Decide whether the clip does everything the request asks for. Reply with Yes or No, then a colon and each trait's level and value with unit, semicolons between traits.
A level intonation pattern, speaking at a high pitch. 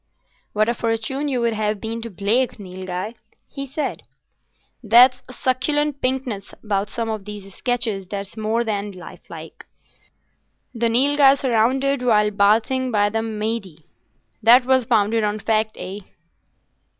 No: average, 3.5 semitones; high, 225 Hz